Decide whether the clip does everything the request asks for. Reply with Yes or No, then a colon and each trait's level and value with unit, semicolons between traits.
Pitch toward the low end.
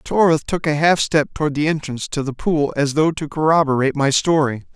No: medium, 150 Hz